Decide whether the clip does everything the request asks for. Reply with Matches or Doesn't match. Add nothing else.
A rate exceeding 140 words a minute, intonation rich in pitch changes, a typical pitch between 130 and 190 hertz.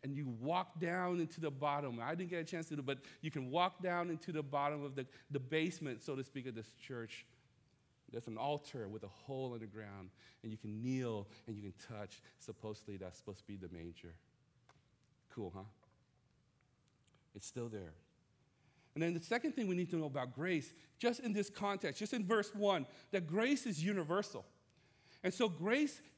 Matches